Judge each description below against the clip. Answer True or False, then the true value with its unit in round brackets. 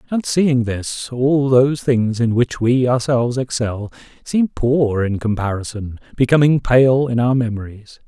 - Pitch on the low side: True (125 Hz)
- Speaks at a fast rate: False (150 wpm)